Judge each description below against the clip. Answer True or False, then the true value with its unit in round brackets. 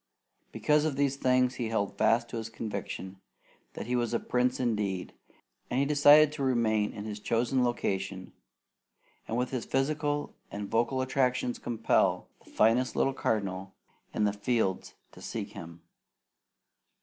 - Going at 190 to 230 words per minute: False (150 wpm)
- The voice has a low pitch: True (120 Hz)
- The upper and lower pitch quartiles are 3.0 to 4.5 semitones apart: True (3.9 semitones)